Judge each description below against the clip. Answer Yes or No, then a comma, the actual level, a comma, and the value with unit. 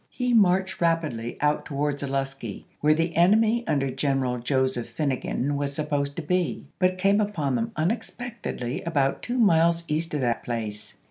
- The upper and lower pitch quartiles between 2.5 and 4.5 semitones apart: No, average, 5.0 semitones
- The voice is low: No, medium, 150 Hz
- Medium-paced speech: Yes, average, 160 wpm